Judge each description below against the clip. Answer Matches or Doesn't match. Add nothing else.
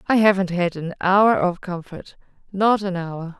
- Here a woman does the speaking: Matches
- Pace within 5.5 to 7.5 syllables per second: Doesn't match